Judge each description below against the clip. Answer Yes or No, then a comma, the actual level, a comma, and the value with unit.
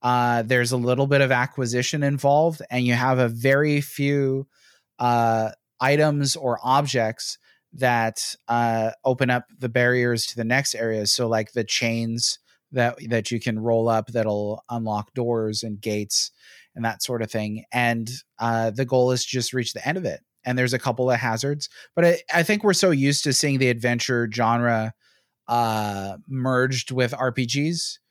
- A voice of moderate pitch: No, low, 125 Hz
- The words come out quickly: No, average, 175 wpm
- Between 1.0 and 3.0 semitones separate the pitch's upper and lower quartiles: Yes, narrow, 2.6 semitones